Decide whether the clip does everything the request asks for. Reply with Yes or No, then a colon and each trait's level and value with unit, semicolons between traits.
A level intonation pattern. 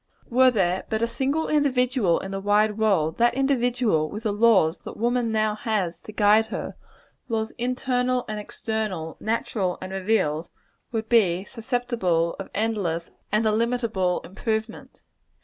No: average, 3.8 semitones